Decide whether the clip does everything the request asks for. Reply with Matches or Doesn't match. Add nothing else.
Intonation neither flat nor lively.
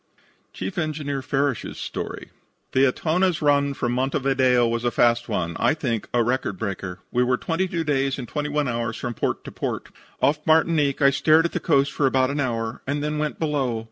Matches